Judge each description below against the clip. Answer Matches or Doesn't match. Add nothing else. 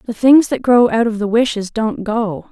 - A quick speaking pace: Matches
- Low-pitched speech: Doesn't match